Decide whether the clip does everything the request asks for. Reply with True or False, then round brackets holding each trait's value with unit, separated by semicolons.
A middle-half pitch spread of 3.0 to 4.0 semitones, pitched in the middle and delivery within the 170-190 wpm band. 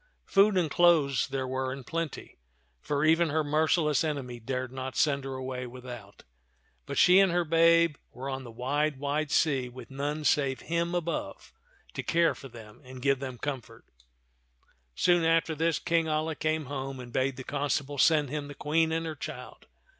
True (3.6 semitones; 145 Hz; 180 wpm)